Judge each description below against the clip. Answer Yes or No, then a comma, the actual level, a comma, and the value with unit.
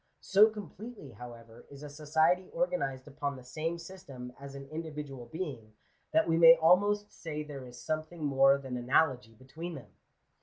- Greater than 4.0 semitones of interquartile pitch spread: Yes, average, 4.4 semitones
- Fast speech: No, average, 165 wpm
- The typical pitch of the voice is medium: Yes, medium, 150 Hz